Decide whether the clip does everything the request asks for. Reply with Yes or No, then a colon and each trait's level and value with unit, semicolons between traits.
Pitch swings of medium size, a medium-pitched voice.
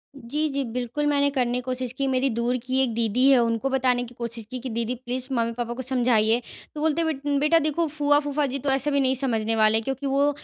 No: average, 3.0 semitones; very high, 255 Hz